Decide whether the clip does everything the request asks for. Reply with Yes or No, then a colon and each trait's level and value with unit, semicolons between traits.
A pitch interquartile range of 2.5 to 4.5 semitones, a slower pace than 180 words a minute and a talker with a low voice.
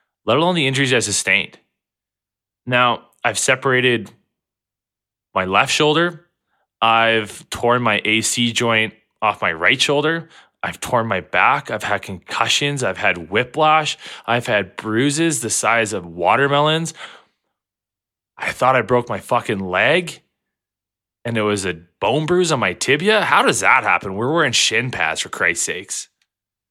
No: average, 5.3 semitones; average, 145 wpm; low, 115 Hz